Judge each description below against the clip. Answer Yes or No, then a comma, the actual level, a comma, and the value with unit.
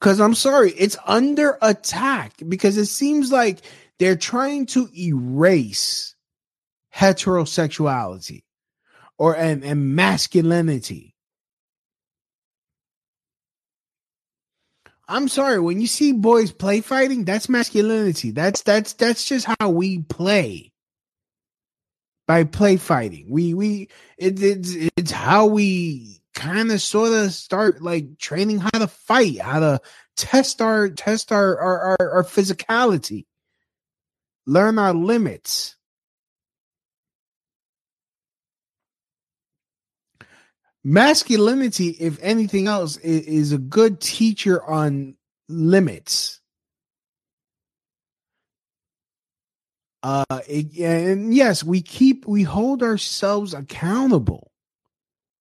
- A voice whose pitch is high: Yes, high, 195 Hz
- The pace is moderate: No, slow, 95 wpm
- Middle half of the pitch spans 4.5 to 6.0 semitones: Yes, average, 5.2 semitones